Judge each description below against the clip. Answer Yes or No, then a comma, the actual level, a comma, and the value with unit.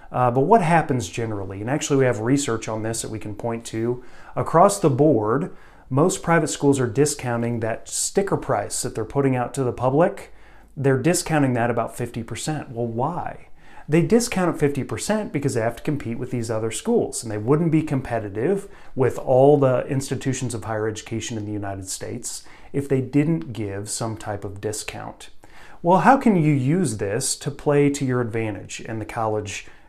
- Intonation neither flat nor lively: Yes, average, 4.5 semitones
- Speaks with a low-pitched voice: Yes, low, 125 Hz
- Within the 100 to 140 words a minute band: No, average, 185 wpm